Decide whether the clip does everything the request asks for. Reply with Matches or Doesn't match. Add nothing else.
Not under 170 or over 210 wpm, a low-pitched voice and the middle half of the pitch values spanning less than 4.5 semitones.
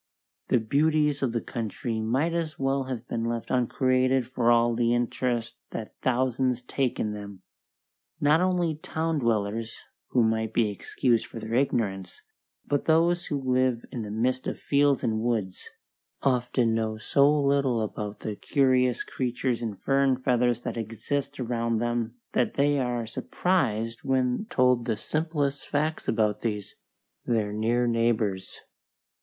Doesn't match